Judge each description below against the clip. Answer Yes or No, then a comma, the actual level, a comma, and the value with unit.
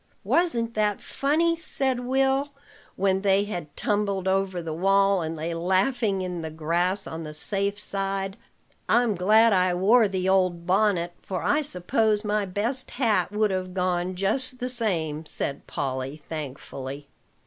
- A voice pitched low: No, high, 195 Hz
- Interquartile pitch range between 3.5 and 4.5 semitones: Yes, average, 3.8 semitones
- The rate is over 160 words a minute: No, average, 150 wpm